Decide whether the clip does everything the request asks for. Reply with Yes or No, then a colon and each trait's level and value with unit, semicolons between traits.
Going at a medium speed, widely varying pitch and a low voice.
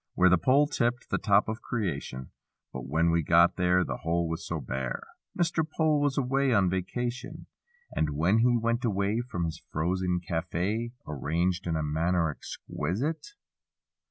Yes: average, 160 wpm; wide, 6.5 semitones; very low, 90 Hz